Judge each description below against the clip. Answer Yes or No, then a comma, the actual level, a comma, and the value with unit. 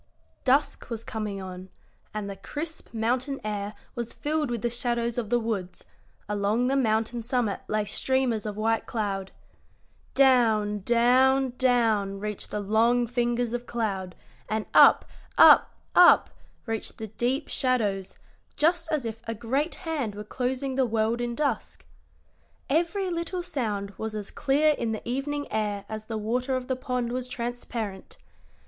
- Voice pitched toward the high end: Yes, high, 235 Hz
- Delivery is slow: No, average, 155 wpm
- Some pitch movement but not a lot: Yes, average, 3.4 semitones